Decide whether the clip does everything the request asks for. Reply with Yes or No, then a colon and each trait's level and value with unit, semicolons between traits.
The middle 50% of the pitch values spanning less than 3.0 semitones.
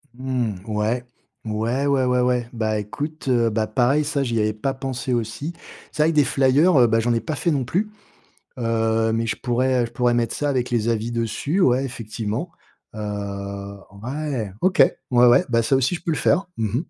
No: average, 3.3 semitones